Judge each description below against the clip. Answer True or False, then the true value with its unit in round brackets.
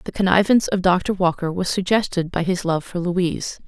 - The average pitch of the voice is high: False (180 Hz)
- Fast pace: False (195 wpm)